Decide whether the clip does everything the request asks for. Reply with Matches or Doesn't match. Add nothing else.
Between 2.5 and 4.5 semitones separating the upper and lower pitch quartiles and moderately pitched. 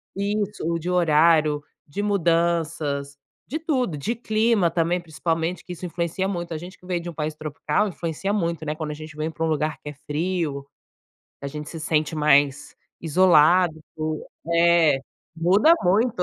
Matches